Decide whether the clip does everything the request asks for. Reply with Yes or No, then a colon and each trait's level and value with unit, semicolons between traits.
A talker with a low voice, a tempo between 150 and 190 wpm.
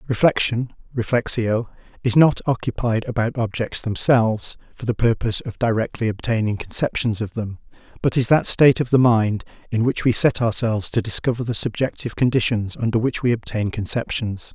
Yes: low, 115 Hz; average, 160 wpm